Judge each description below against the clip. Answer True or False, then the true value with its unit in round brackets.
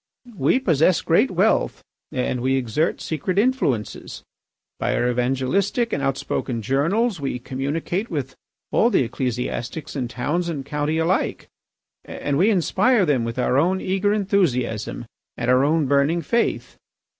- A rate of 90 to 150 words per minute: True (140 wpm)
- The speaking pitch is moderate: True (145 Hz)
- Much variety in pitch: True (6.4 semitones)